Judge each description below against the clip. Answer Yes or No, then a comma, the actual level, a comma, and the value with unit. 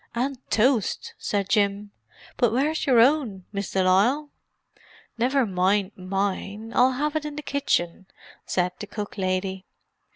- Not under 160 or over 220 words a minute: No, slow, 135 wpm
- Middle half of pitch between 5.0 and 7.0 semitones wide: Yes, wide, 5.5 semitones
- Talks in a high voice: Yes, high, 210 Hz